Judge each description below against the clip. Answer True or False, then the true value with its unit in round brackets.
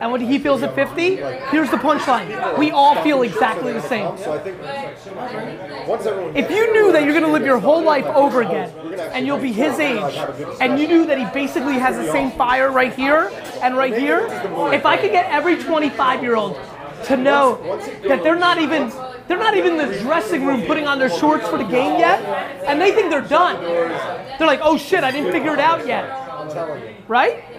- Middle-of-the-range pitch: False (285 Hz)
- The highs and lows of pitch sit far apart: False (3.4 semitones)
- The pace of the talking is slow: False (195 wpm)